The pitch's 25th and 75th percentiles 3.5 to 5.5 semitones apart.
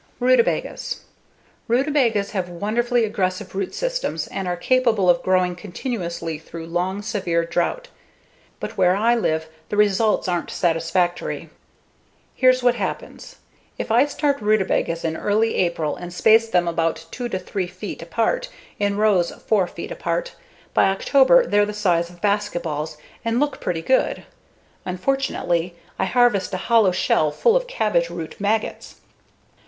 Yes: average, 5.0 semitones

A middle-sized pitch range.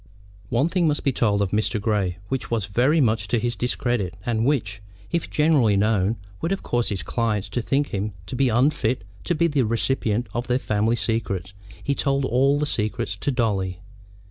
Yes: average, 4.5 semitones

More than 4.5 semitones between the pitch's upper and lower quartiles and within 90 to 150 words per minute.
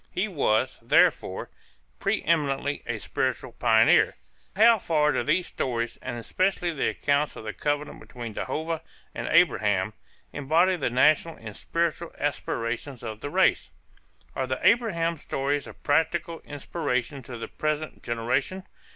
Yes: wide, 5.6 semitones; average, 140 wpm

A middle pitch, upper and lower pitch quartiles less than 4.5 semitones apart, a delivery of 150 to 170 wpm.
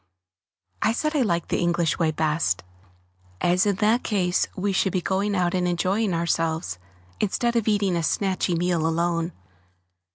Yes: medium, 180 Hz; average, 3.3 semitones; average, 160 wpm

